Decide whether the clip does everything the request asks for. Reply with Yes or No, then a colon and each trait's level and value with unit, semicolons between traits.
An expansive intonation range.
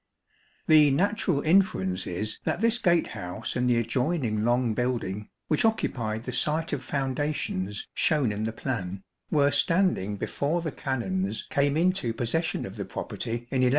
Yes: wide, 6.2 semitones